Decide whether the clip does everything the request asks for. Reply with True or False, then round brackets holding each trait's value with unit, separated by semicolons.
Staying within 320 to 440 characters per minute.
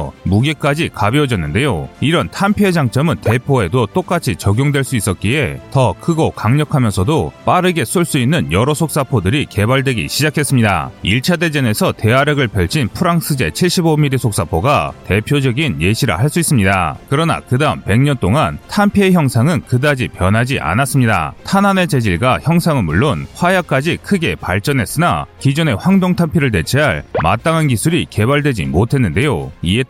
True (355 characters per minute)